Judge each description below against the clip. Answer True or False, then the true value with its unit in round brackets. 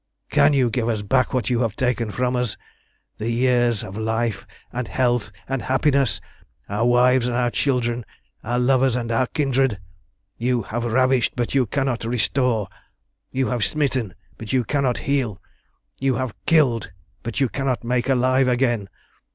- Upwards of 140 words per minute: True (160 wpm)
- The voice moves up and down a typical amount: False (2.0 semitones)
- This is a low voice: True (125 Hz)